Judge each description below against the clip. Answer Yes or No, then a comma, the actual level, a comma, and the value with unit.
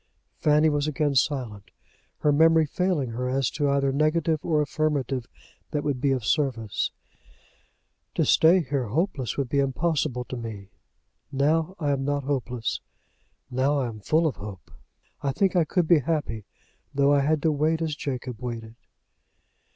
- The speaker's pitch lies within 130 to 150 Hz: Yes, medium, 140 Hz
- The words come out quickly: No, average, 160 wpm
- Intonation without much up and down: No, average, 3.6 semitones